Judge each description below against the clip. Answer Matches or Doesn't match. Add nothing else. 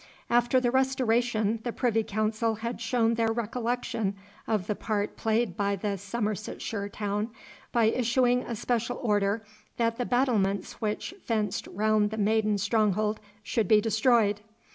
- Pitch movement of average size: Doesn't match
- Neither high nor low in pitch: Doesn't match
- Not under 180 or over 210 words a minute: Doesn't match